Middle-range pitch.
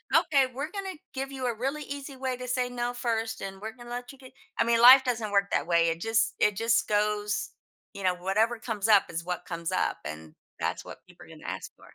No: high, 230 Hz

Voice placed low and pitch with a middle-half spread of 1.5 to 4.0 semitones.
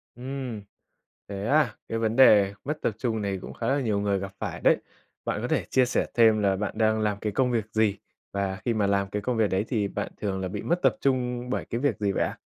Yes: low, 110 Hz; average, 3.6 semitones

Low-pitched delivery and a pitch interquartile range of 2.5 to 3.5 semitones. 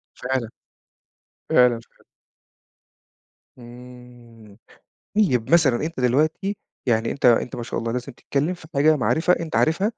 No: low, 125 Hz; average, 4.8 semitones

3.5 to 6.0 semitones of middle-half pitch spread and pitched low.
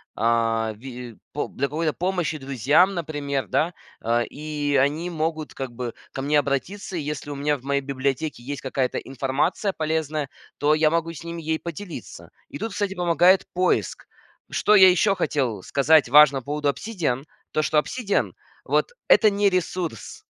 No: average, 3.9 semitones; medium, 150 Hz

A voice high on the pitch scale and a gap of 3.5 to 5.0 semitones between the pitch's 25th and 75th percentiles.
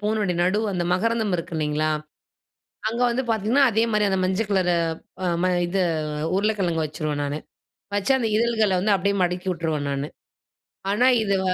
Yes: high, 195 Hz; average, 4.1 semitones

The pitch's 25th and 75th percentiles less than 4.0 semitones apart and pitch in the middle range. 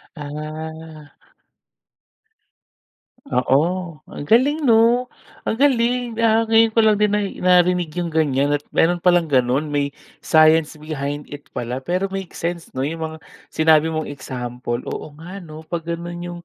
No: average, 4.3 semitones; medium, 160 Hz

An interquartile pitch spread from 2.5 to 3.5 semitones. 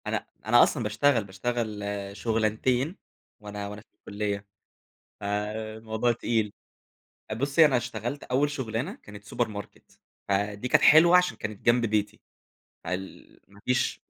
Yes: average, 3.2 semitones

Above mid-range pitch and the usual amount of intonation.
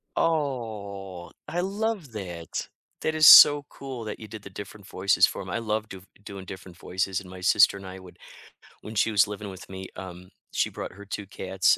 No: low, 100 Hz; average, 3.2 semitones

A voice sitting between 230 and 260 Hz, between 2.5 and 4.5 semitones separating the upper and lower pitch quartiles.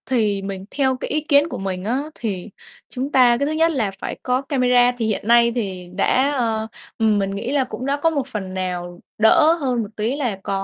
No: high, 240 Hz; average, 5.2 semitones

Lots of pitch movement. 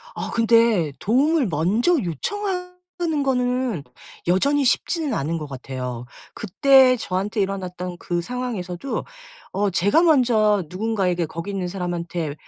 Yes: wide, 6.7 semitones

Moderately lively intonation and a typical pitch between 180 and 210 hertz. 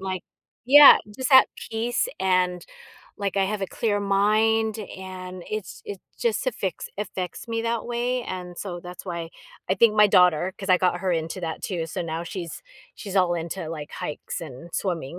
Yes: average, 3.4 semitones; high, 190 Hz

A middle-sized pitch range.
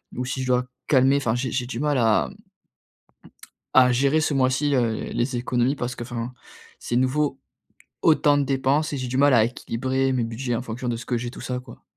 No: narrow, 2.0 semitones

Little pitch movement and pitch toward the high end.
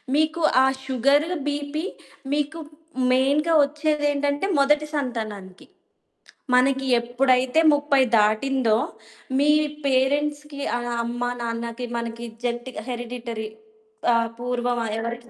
No: average, 3.6 semitones; very high, 260 Hz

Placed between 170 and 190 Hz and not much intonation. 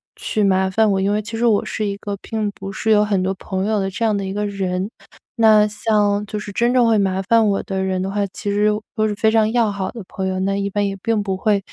No: high, 205 Hz; narrow, 1.9 semitones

